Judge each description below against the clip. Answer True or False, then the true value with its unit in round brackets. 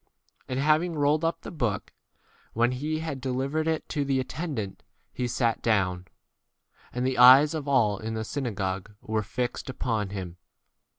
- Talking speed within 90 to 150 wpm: False (165 wpm)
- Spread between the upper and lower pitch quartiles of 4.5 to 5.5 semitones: True (5.2 semitones)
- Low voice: True (125 Hz)